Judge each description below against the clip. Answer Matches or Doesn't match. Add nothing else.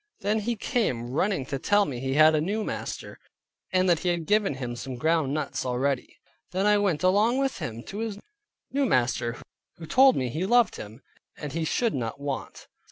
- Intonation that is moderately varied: Doesn't match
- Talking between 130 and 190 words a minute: Doesn't match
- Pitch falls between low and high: Matches